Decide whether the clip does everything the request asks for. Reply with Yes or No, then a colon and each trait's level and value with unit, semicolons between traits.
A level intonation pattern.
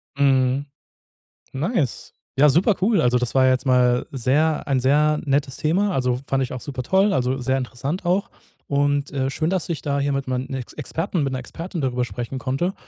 No: average, 3.1 semitones